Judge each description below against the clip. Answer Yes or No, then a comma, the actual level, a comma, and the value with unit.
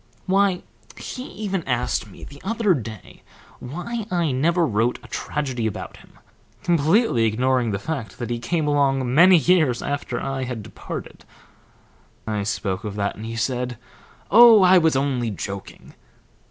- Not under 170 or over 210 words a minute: No, average, 155 wpm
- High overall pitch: No, low, 135 Hz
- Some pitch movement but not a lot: No, wide, 7.3 semitones